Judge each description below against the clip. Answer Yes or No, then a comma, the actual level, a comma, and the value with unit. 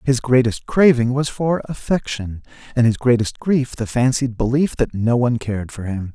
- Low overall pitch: Yes, low, 125 Hz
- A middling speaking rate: Yes, average, 185 wpm